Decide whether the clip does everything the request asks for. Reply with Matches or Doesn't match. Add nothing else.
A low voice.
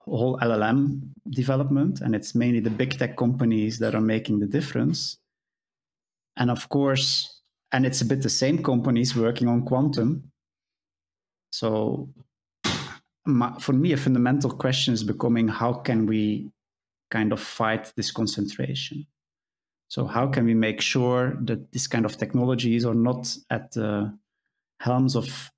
Matches